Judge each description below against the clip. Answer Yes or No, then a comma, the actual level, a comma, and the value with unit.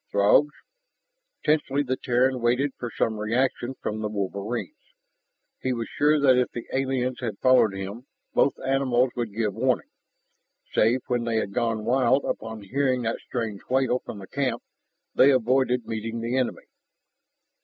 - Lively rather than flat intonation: No, average, 2.9 semitones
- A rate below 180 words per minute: Yes, average, 155 wpm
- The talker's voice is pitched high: No, low, 125 Hz